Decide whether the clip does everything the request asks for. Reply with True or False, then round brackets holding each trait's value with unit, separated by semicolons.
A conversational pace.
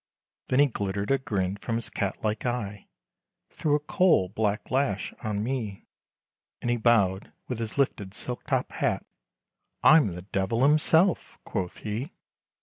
True (150 wpm)